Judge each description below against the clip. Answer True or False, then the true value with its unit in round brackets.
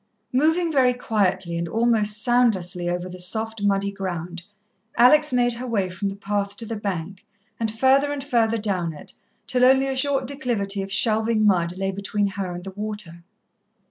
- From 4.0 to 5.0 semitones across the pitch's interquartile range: True (4.4 semitones)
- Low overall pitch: False (210 Hz)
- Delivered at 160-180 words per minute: True (175 wpm)